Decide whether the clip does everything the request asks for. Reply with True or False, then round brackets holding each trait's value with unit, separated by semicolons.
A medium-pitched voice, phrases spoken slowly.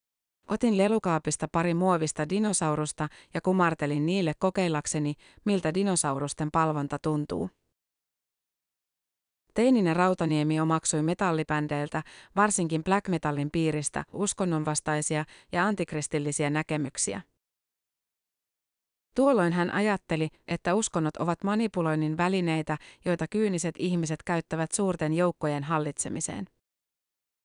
True (160 Hz; 85 wpm)